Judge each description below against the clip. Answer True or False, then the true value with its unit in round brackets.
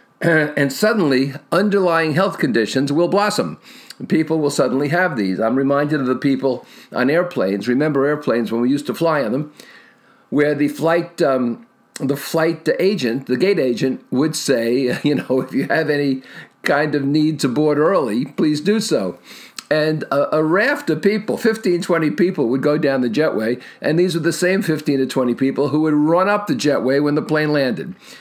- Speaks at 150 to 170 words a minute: False (185 wpm)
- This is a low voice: False (150 Hz)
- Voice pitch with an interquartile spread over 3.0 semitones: True (3.9 semitones)